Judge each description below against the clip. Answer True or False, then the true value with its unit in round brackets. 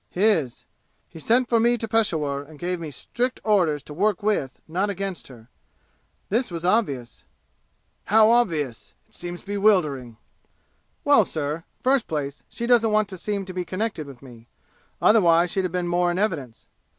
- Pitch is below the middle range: False (180 Hz)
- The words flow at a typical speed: True (165 wpm)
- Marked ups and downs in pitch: True (6.1 semitones)